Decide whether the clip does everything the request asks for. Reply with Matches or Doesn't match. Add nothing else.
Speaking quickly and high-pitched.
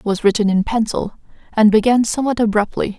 Doesn't match